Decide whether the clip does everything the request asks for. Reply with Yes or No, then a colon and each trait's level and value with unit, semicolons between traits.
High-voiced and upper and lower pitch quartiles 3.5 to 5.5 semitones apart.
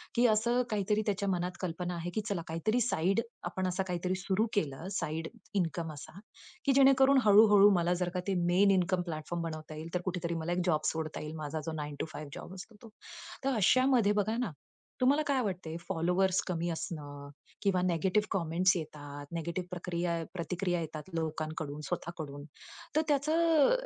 No: medium, 180 Hz; average, 4.0 semitones